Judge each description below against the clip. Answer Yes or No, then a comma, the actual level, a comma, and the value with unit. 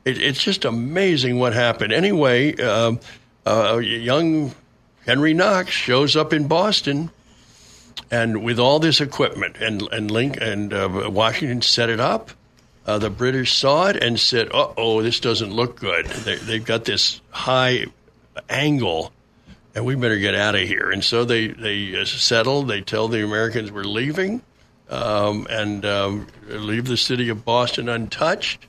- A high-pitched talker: No, low, 115 Hz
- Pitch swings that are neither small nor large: Yes, average, 3.0 semitones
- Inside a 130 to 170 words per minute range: Yes, average, 160 wpm